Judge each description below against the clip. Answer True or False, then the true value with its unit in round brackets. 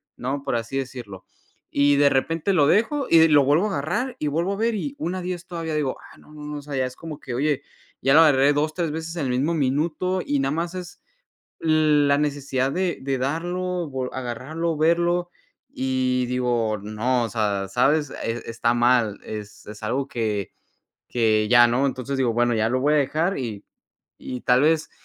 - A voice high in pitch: False (140 Hz)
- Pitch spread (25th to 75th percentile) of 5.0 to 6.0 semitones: False (4.6 semitones)